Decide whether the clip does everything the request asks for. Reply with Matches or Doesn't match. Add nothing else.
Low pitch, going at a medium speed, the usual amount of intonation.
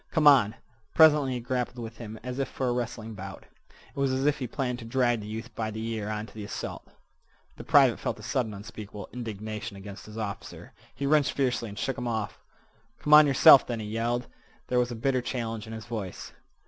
Doesn't match